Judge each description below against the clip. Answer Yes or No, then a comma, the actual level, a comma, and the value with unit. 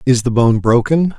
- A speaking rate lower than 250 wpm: Yes, fast, 205 wpm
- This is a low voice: Yes, low, 125 Hz